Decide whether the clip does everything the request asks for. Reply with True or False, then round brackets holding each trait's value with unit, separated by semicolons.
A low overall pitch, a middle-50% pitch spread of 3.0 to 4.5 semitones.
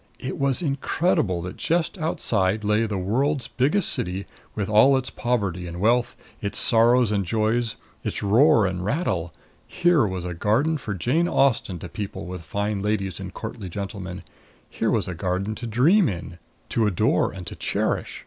False (105 Hz; 5.3 semitones)